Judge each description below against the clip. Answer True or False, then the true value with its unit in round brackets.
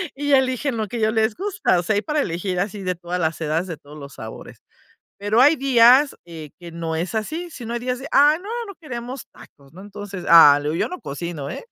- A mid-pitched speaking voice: False (205 Hz)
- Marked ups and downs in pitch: True (7.6 semitones)